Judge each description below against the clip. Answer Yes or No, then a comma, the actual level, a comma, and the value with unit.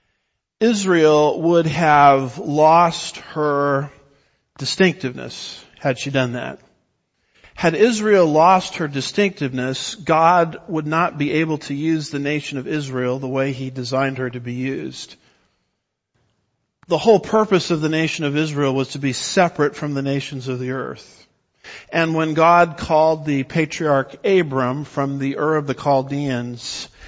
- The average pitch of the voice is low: No, medium, 145 Hz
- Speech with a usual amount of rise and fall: Yes, average, 3.4 semitones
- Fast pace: No, average, 145 wpm